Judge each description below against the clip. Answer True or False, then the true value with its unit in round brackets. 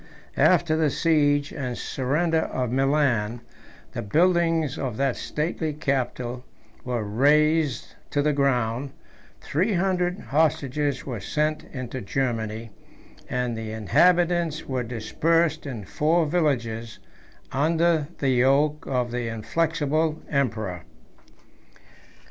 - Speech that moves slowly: True (110 wpm)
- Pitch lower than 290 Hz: True (140 Hz)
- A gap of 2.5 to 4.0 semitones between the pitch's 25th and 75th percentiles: False (4.5 semitones)